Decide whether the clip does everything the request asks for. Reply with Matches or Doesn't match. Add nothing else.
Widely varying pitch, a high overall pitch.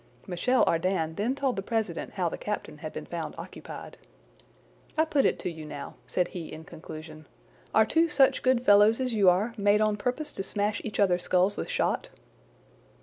Matches